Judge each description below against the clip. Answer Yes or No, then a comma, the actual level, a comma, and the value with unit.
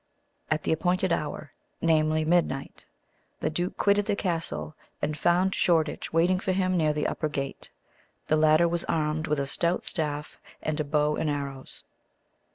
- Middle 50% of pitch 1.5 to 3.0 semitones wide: Yes, narrow, 2.5 semitones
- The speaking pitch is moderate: Yes, medium, 155 Hz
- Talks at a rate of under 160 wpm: No, average, 165 wpm